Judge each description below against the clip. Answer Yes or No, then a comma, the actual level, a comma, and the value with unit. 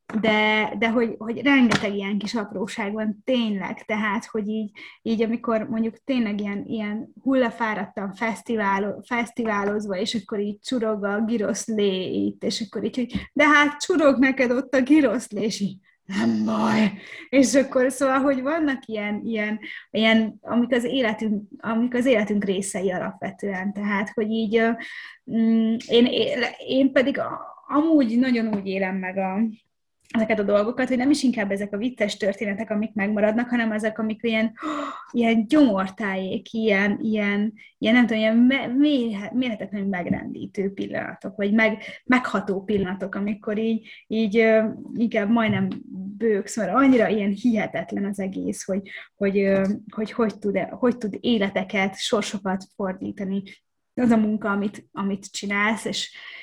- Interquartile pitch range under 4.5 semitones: Yes, average, 2.8 semitones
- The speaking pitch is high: Yes, high, 220 Hz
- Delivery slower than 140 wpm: No, average, 145 wpm